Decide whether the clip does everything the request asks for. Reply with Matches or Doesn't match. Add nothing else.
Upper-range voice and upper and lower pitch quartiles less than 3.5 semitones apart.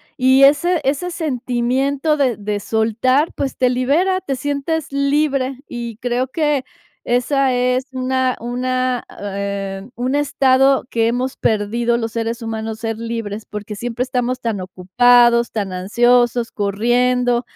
Matches